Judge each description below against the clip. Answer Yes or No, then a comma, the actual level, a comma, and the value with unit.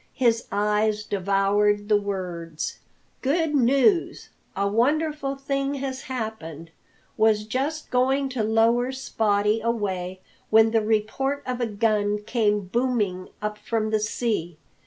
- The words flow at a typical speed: No, slow, 125 wpm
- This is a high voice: Yes, high, 220 Hz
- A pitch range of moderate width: Yes, average, 4.0 semitones